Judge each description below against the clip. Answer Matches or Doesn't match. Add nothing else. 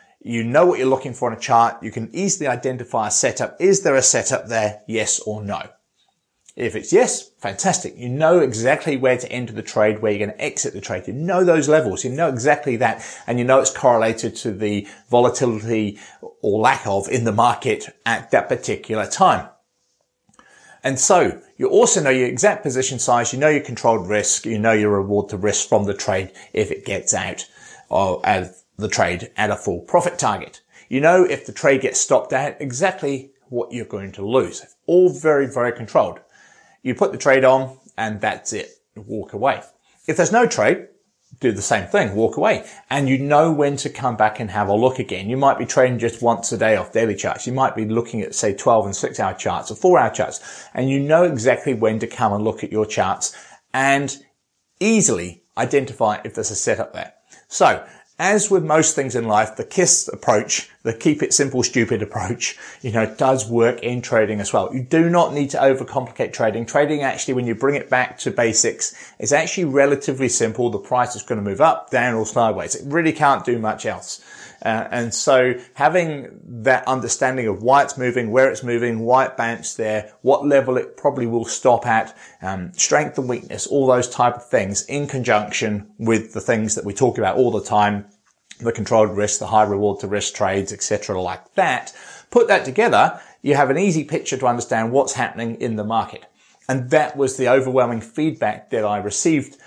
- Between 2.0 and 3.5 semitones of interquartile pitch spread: Doesn't match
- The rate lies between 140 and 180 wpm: Doesn't match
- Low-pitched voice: Matches